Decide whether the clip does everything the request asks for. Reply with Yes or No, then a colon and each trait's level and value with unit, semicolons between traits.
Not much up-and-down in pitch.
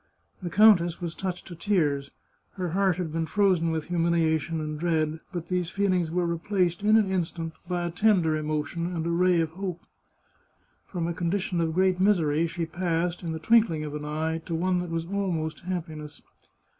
Yes: narrow, 2.2 semitones